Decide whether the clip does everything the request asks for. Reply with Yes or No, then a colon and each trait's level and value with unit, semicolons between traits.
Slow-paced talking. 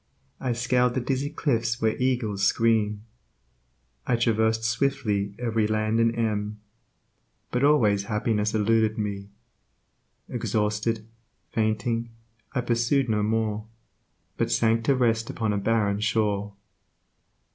Yes: slow, 115 wpm